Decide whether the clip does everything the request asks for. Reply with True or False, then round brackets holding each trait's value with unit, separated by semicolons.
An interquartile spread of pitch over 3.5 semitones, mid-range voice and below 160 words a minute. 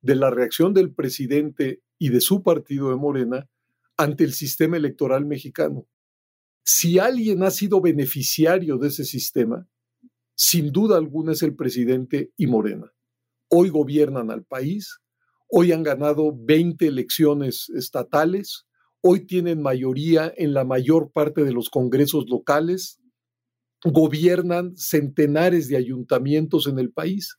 True (4.5 semitones; 150 Hz; 130 wpm)